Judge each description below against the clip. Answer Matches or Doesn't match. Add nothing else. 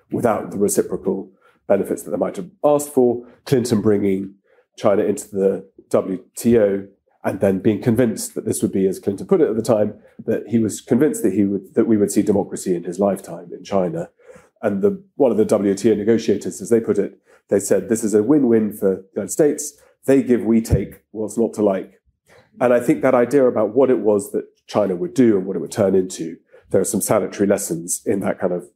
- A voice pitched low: Matches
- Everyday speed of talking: Doesn't match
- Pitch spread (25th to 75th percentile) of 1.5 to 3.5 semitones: Doesn't match